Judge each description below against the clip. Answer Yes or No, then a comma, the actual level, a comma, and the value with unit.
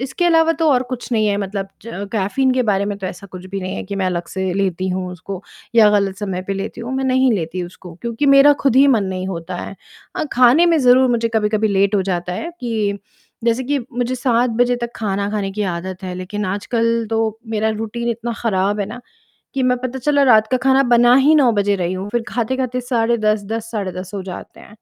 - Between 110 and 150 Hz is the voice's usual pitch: No, high, 215 Hz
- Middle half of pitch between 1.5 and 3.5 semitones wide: No, average, 4.2 semitones